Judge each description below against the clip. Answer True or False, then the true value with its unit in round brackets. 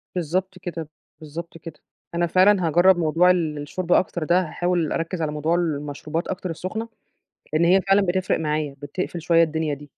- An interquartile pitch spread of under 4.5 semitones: True (2.8 semitones)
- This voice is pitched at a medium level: True (170 Hz)